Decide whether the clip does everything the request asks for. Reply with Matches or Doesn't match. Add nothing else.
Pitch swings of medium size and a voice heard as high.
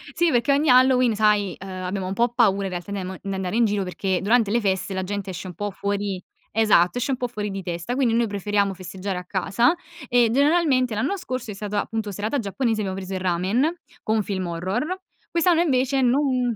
Matches